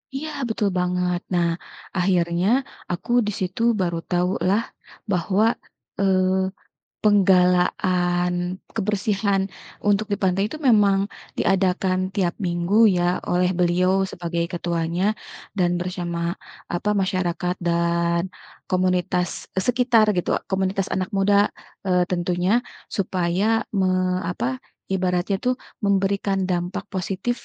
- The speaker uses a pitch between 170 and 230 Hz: Yes, medium, 185 Hz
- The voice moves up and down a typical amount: No, narrow, 1.8 semitones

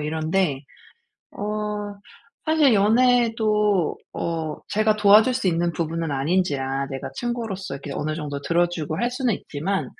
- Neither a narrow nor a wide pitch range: No, wide, 5.9 semitones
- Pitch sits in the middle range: Yes, medium, 180 Hz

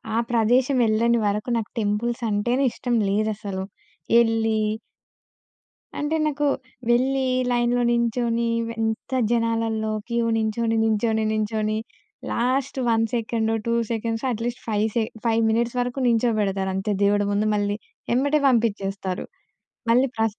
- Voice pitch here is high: Yes, high, 225 Hz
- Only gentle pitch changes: Yes, narrow, 1.8 semitones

